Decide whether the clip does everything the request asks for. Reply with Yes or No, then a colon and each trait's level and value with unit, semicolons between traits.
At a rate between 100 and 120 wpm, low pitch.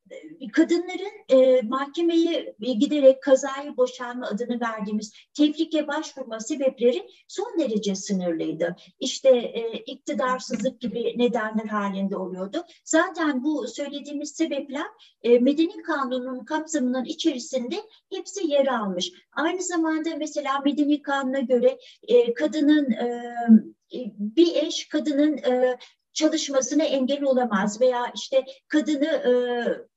No: average, 105 wpm; very high, 270 Hz